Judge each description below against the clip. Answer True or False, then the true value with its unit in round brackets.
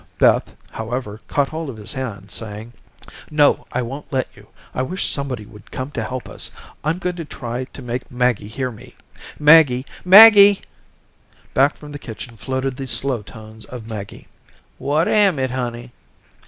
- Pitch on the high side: False (130 Hz)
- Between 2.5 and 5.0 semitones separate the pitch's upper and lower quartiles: True (4.1 semitones)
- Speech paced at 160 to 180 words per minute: True (170 wpm)